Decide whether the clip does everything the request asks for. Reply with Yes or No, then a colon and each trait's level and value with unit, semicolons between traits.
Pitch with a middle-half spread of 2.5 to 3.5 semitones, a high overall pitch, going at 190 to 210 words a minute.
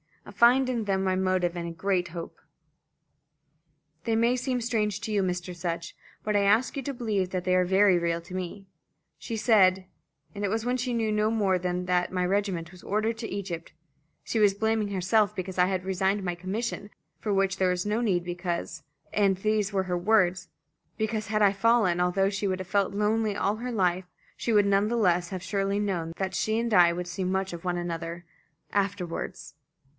Yes: average, 3.0 semitones; high, 195 Hz; fast, 205 wpm